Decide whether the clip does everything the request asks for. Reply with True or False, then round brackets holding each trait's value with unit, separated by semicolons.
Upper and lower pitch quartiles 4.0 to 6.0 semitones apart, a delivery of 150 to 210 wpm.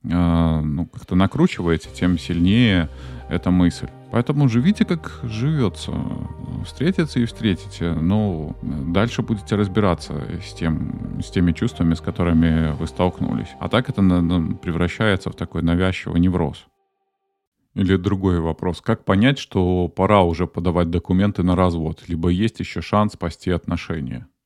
False (4.4 semitones; 130 wpm)